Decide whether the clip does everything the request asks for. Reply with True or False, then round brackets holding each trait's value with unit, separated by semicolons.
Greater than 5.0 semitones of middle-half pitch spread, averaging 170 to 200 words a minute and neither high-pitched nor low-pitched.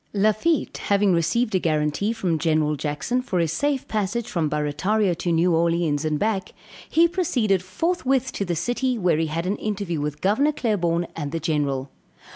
True (5.6 semitones; 175 wpm; 180 Hz)